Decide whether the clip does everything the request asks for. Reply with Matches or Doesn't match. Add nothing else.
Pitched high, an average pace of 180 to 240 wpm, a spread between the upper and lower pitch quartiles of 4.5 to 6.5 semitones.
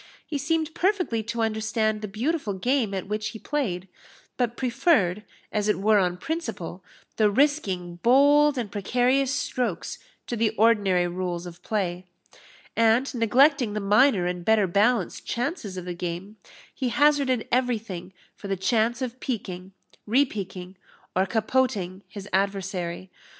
Doesn't match